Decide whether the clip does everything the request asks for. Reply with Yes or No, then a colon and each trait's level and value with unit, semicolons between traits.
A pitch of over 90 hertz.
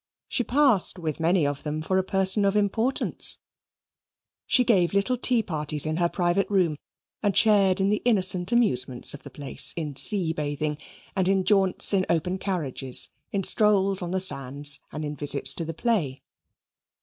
Yes: medium, 185 Hz